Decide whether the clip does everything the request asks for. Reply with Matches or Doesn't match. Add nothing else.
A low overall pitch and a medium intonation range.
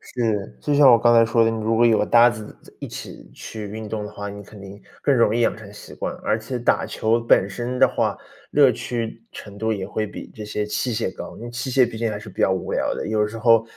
Doesn't match